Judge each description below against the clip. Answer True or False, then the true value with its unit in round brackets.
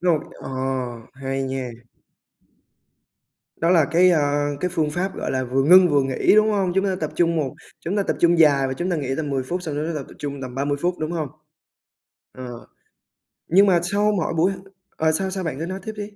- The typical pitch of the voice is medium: True (160 Hz)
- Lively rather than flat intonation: False (4.6 semitones)